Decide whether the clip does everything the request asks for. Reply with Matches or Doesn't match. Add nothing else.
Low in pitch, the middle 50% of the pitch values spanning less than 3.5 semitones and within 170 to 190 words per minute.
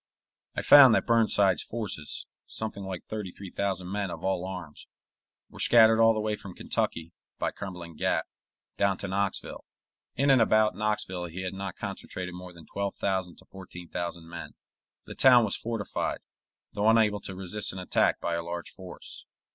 Matches